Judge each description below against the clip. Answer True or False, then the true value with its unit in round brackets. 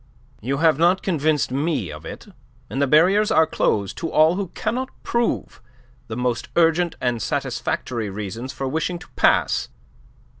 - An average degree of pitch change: False (5.7 semitones)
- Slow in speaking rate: False (155 wpm)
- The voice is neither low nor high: True (155 Hz)